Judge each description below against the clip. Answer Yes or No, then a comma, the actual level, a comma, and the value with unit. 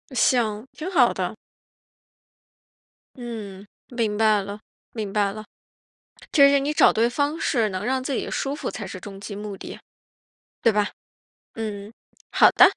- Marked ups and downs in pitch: No, average, 3.8 semitones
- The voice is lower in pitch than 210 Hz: No, high, 220 Hz